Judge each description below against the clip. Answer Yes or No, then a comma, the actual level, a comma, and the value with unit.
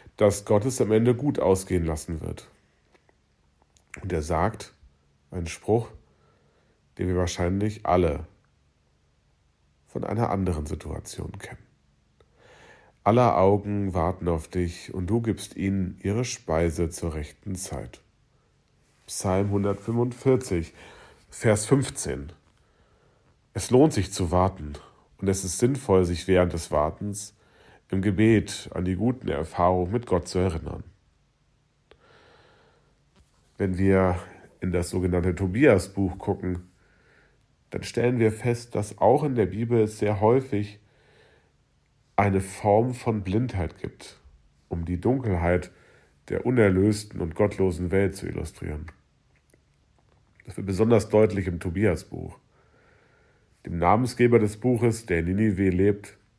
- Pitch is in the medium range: No, very low, 95 Hz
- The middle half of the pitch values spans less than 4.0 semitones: Yes, average, 3.4 semitones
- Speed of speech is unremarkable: No, slow, 120 wpm